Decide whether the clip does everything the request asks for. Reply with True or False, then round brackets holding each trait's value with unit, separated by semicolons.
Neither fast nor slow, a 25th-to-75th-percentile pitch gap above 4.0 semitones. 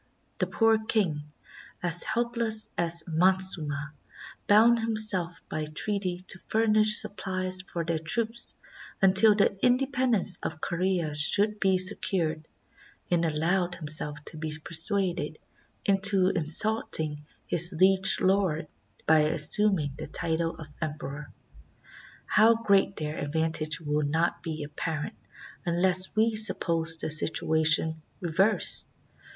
False (120 wpm; 4.5 semitones)